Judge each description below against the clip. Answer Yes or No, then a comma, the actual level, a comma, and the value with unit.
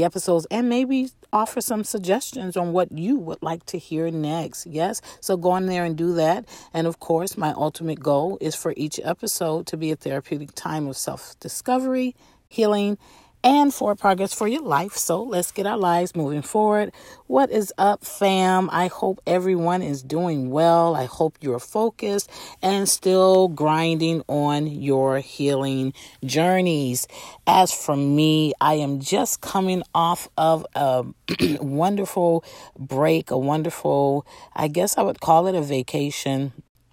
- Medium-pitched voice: Yes, medium, 170 Hz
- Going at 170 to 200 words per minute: No, average, 160 wpm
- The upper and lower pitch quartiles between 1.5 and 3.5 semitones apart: No, average, 4.3 semitones